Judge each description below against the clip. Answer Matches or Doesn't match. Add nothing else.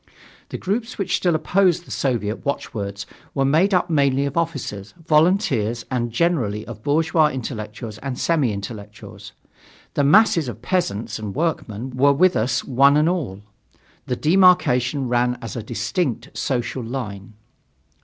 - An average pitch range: Doesn't match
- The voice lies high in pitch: Doesn't match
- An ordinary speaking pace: Matches